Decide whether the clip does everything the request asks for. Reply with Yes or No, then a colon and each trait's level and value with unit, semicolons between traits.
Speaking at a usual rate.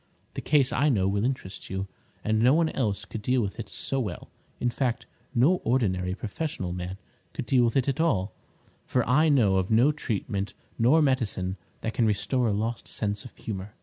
Yes: average, 195 wpm